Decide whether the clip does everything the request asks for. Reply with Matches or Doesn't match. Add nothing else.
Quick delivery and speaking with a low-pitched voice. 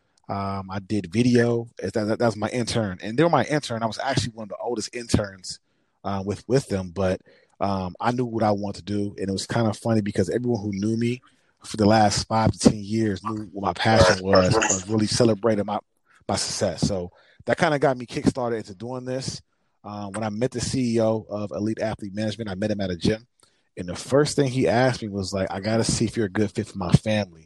Matches